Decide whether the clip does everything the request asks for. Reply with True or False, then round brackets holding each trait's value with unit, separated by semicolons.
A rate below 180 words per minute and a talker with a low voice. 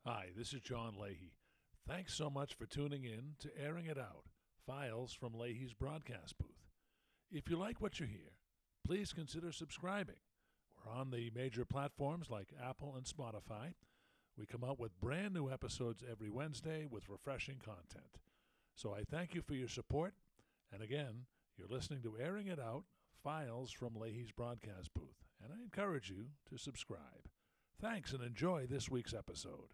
True (165 wpm; 130 Hz)